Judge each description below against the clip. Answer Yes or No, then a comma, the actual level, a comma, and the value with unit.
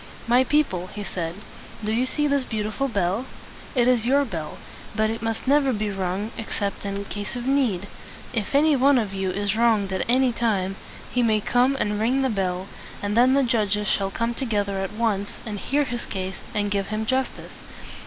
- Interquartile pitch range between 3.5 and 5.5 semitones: Yes, average, 4.0 semitones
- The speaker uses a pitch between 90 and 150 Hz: No, high, 220 Hz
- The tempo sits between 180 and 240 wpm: Yes, average, 195 wpm